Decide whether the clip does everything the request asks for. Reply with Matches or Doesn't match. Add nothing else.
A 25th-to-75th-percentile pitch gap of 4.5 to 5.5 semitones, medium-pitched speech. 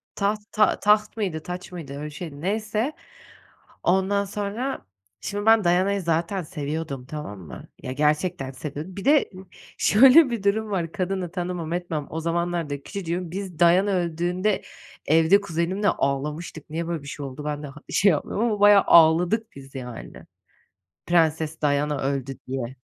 Matches